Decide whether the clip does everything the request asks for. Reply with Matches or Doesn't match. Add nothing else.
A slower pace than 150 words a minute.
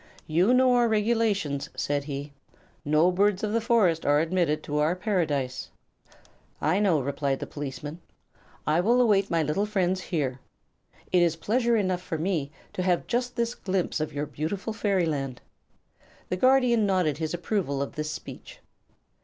Doesn't match